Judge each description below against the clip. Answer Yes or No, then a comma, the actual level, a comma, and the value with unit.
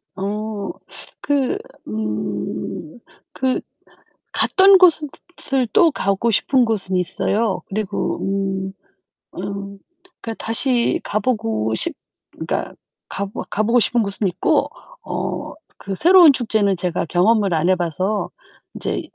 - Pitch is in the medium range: No, high, 205 Hz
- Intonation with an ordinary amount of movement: Yes, average, 3.9 semitones